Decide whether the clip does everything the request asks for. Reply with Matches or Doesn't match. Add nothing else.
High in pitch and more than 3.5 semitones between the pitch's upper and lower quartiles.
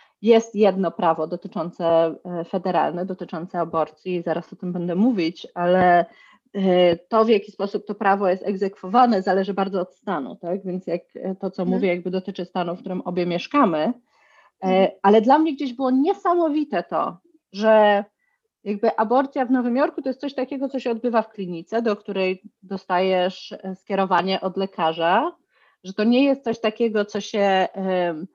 Matches